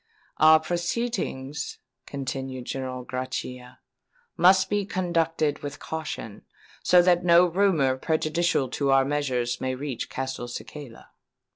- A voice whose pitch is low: No, medium, 145 Hz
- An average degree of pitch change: Yes, average, 4.8 semitones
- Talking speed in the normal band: No, slow, 110 wpm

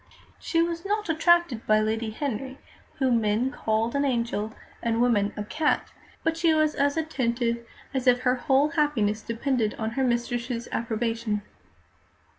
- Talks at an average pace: Yes, average, 150 wpm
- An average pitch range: Yes, average, 4.4 semitones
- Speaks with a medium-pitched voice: No, high, 245 Hz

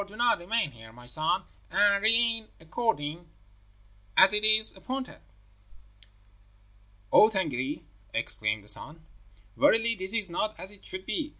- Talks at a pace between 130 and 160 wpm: Yes, slow, 135 wpm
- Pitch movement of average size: No, wide, 6.4 semitones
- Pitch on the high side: Yes, high, 195 Hz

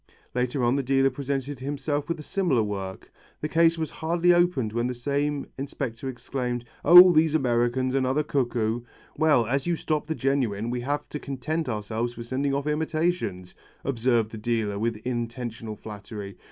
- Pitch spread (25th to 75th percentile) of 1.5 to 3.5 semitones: No, average, 4.0 semitones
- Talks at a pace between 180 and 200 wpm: No, average, 165 wpm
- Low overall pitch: Yes, low, 130 Hz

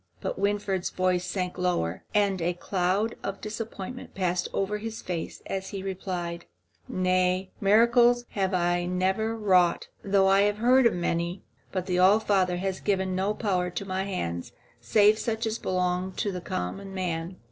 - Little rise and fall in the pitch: Yes, narrow, 2.3 semitones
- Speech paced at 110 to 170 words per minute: Yes, average, 160 wpm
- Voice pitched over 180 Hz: Yes, high, 190 Hz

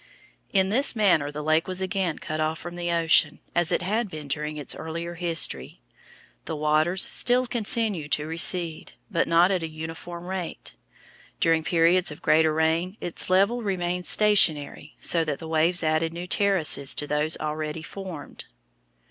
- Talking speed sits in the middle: Yes, average, 165 wpm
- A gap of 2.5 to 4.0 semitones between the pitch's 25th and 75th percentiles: Yes, average, 2.8 semitones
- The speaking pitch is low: No, medium, 165 Hz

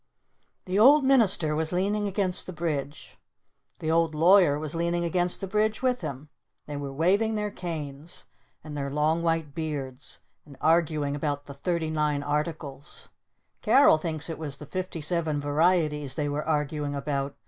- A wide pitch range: No, average, 3.4 semitones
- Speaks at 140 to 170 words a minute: Yes, average, 160 wpm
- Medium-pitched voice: Yes, medium, 155 Hz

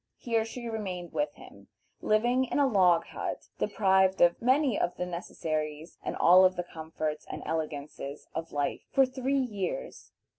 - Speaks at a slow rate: No, average, 160 wpm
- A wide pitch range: Yes, wide, 7.0 semitones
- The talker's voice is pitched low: No, medium, 185 Hz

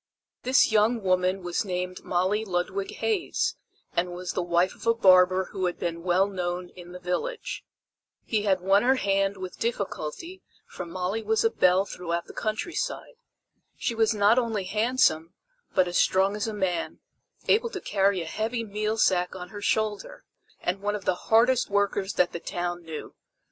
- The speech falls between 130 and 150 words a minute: No, average, 175 wpm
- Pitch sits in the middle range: No, high, 195 Hz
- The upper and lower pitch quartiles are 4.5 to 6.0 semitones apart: No, average, 3.6 semitones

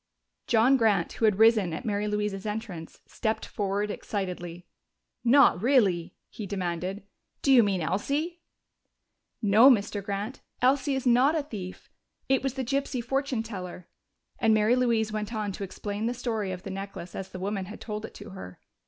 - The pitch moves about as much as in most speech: Yes, average, 4.0 semitones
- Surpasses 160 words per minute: Yes, average, 170 wpm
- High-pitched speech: Yes, high, 210 Hz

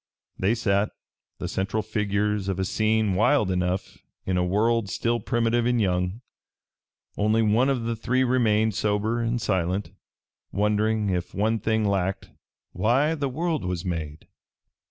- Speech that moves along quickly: No, average, 145 wpm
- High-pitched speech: No, low, 105 Hz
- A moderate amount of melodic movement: Yes, average, 3.3 semitones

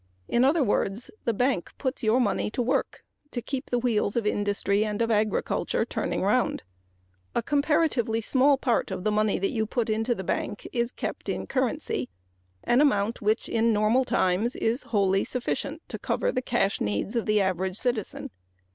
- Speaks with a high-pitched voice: Yes, high, 225 Hz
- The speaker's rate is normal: Yes, average, 175 wpm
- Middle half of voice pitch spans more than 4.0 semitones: No, average, 3.5 semitones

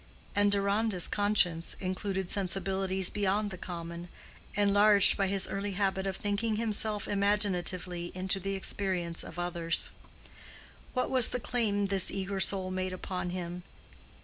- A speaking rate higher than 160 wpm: No, slow, 135 wpm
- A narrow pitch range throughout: Yes, narrow, 1.9 semitones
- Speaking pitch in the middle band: No, high, 195 Hz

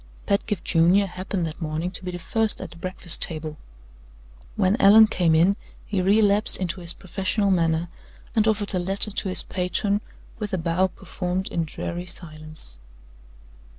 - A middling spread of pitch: Yes, average, 3.0 semitones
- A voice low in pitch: No, medium, 185 Hz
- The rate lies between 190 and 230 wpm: No, average, 160 wpm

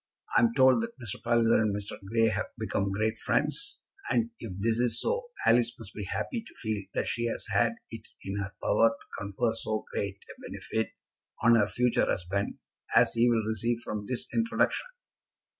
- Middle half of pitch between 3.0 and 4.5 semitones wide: No, narrow, 2.5 semitones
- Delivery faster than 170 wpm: Yes, average, 185 wpm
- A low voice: Yes, low, 115 Hz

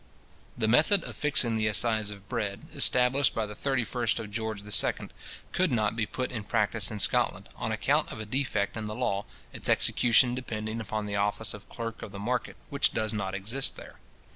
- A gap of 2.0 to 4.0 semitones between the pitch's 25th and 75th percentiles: Yes, average, 2.8 semitones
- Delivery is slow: No, average, 195 wpm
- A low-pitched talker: Yes, low, 110 Hz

